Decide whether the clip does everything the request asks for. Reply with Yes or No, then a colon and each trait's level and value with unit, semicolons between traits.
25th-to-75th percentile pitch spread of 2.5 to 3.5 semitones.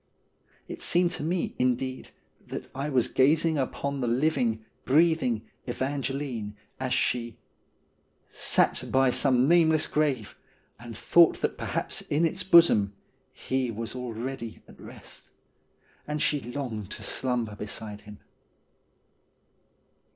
No: average, 4.3 semitones